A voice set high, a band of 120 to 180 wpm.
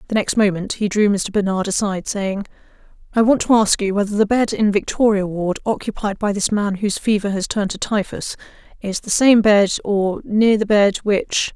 No: high, 205 Hz; fast, 205 wpm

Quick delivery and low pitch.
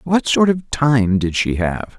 Yes: fast, 210 wpm; low, 125 Hz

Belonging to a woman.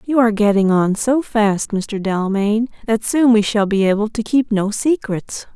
Yes: female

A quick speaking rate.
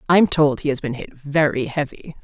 Yes: fast, 215 wpm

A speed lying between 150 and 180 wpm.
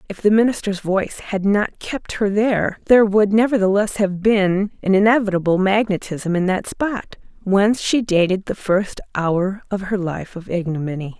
Yes: average, 165 wpm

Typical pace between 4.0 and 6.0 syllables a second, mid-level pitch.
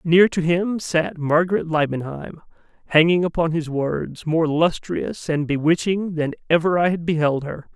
Yes: 4.5 syllables/s; medium, 165 Hz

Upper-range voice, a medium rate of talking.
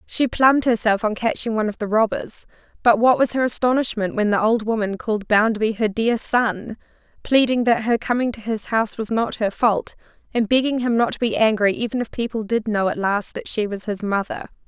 No: high, 220 Hz; fast, 215 wpm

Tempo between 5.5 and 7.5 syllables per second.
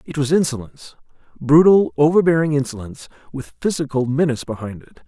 Yes: 6.5 syllables/s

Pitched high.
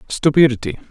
No: low, 125 Hz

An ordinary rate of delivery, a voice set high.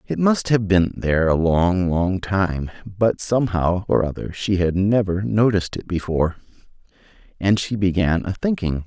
No: average, 160 wpm; very low, 95 Hz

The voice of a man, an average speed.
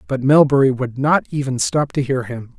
No: male; fast, 210 wpm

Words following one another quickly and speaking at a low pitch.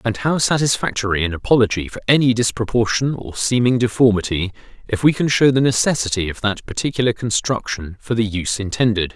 No: average, 165 wpm; low, 115 Hz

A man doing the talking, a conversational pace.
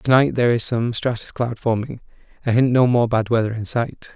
No: male; fast, 215 wpm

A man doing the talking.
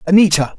Yes: male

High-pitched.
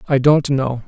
No: medium, 140 Hz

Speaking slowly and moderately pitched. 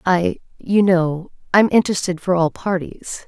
Yes: slow, 110 wpm; medium, 180 Hz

